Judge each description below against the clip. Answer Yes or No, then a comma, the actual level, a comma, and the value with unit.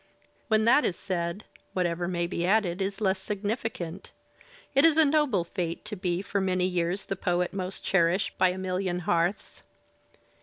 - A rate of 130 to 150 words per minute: No, average, 165 wpm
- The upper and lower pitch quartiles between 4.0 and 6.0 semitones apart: No, average, 2.7 semitones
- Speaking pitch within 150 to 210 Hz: Yes, medium, 185 Hz